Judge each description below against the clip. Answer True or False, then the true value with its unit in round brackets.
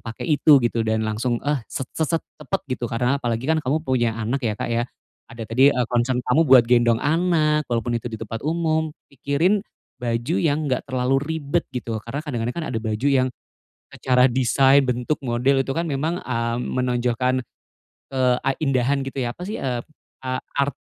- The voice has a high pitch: False (130 Hz)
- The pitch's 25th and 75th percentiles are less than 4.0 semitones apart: True (3.2 semitones)